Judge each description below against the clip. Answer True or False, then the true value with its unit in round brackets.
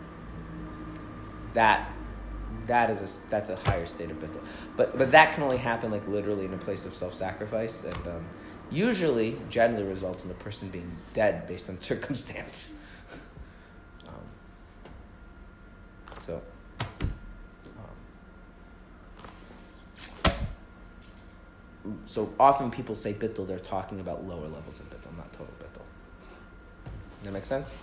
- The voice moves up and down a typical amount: True (3.4 semitones)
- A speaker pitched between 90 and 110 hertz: True (95 Hz)